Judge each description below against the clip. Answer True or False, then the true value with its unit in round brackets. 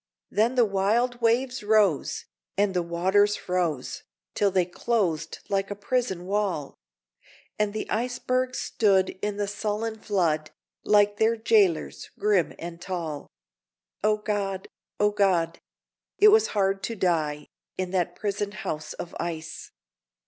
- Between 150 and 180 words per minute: False (135 wpm)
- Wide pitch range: False (3.4 semitones)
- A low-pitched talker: False (200 Hz)